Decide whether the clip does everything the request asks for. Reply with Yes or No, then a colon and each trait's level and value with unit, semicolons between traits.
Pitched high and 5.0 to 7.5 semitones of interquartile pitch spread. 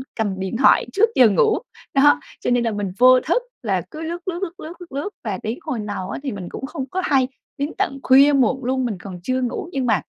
Yes: very high, 260 Hz; wide, 5.4 semitones